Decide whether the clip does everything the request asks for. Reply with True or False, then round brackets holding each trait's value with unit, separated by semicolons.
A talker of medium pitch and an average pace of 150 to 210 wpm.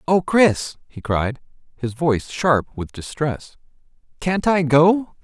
False (150 Hz; 140 wpm)